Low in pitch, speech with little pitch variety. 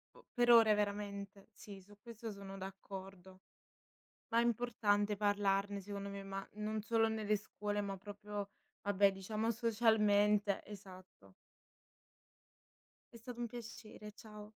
No: high, 205 Hz; narrow, 1.6 semitones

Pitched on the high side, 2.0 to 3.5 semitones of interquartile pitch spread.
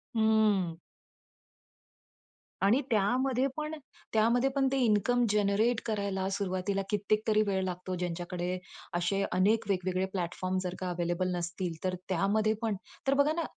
Yes: high, 200 Hz; average, 3.2 semitones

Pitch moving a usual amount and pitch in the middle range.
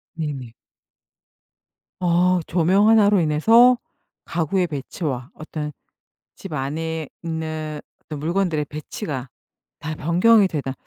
Yes: average, 3.5 semitones; medium, 160 Hz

